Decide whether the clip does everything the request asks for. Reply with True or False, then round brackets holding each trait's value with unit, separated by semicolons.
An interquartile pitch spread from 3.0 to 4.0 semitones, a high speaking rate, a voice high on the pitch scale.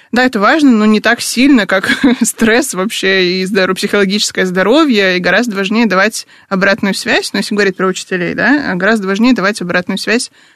True (3.7 semitones; 180 wpm; 205 Hz)